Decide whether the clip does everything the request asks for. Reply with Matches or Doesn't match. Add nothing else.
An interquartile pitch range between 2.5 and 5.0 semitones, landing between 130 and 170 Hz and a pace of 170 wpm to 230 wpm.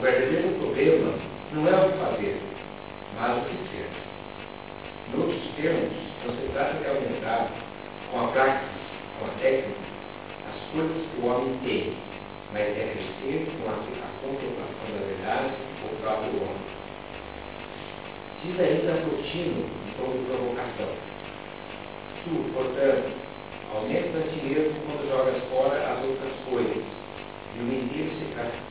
Doesn't match